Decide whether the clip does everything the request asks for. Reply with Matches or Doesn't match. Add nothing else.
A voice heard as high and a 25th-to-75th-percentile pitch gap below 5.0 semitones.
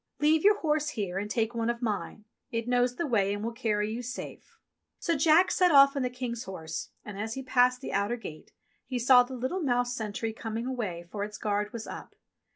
Matches